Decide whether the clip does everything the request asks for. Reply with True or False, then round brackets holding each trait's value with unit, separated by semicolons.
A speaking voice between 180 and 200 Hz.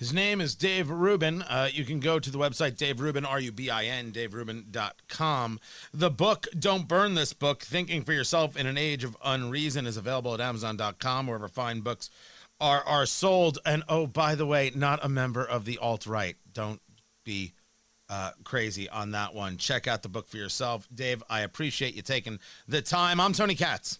False (130 Hz)